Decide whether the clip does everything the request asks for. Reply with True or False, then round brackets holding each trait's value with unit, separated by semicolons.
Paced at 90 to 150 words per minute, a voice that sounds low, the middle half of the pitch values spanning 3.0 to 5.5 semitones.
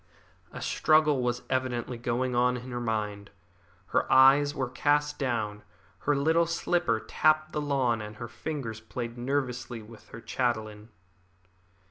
True (140 wpm; 125 Hz; 3.8 semitones)